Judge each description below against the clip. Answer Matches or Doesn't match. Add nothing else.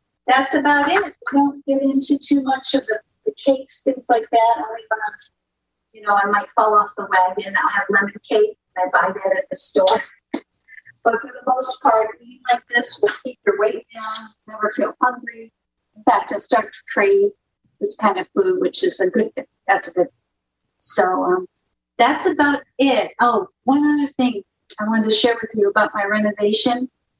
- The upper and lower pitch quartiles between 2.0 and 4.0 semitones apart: Doesn't match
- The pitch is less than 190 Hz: Doesn't match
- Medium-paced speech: Matches